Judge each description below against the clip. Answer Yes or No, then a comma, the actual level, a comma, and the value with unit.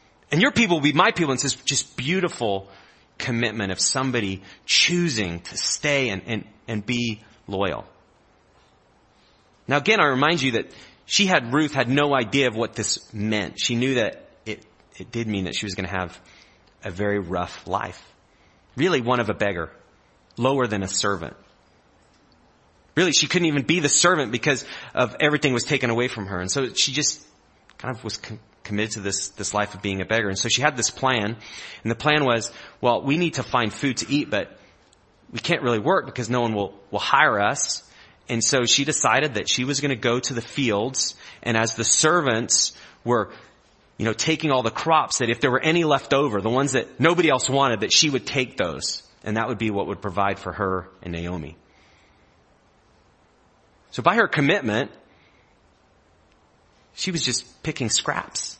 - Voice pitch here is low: Yes, low, 115 Hz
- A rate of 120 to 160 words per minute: No, average, 195 wpm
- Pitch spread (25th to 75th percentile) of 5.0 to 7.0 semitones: Yes, wide, 5.5 semitones